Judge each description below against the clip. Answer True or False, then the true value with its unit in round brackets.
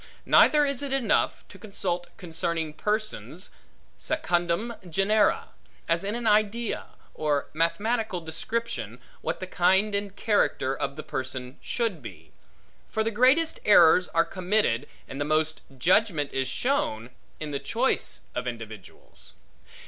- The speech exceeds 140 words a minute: False (135 wpm)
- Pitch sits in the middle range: True (180 Hz)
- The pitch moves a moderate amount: False (6.8 semitones)